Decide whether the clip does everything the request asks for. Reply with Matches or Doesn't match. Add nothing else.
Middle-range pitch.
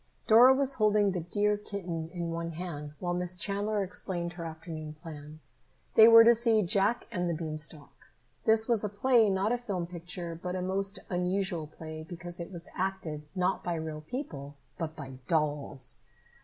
Matches